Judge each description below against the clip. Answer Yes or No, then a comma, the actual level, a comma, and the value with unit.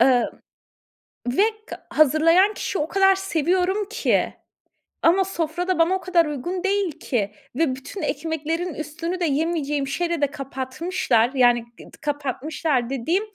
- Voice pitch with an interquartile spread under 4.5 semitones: No, average, 4.8 semitones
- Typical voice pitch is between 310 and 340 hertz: Yes, very high, 320 Hz